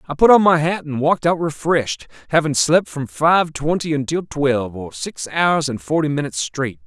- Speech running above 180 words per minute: Yes, average, 200 wpm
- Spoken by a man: Yes, male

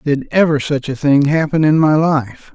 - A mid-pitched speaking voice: Yes, medium, 145 Hz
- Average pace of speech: No, fast, 210 wpm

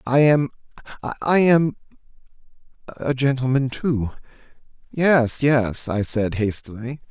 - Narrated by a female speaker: No, male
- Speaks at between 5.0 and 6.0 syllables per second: No, 3.7 syllables/s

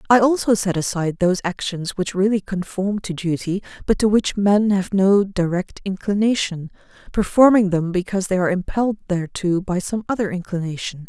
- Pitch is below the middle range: No, high, 190 Hz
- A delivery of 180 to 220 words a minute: No, average, 160 wpm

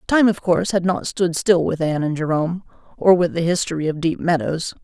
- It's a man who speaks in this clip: No, female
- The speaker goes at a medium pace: No, fast, 225 wpm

